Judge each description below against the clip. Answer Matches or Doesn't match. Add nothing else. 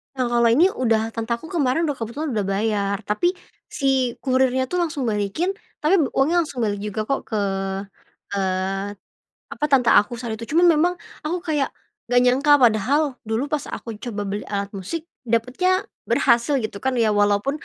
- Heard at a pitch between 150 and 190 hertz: Doesn't match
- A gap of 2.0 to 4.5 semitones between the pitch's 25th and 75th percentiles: Doesn't match